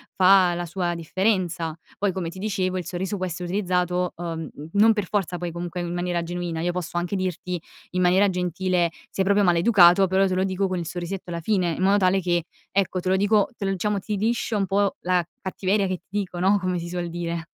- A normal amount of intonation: No, narrow, 1.9 semitones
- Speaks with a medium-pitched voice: Yes, medium, 180 Hz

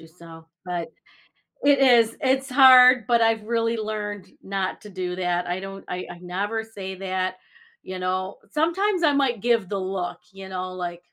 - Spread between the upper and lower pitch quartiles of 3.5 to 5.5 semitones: Yes, average, 4.3 semitones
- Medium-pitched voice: No, high, 195 Hz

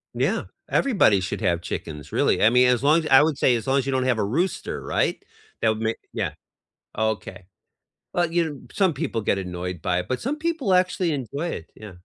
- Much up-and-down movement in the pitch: Yes, wide, 8.5 semitones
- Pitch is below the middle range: Yes, low, 125 Hz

